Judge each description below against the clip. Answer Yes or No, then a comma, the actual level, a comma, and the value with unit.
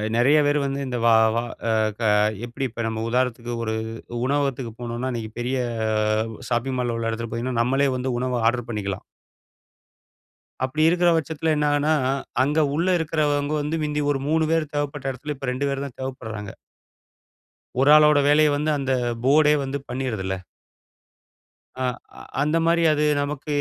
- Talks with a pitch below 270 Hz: Yes, low, 135 Hz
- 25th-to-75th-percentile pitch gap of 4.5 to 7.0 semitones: No, average, 3.7 semitones